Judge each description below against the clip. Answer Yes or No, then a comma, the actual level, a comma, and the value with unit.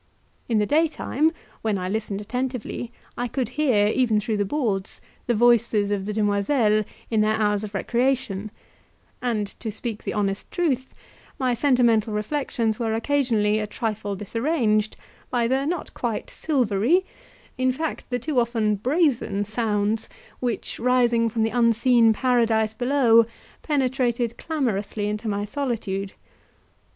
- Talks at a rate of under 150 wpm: Yes, average, 140 wpm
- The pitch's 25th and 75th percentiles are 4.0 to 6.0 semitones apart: No, average, 3.3 semitones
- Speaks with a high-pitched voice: Yes, high, 230 Hz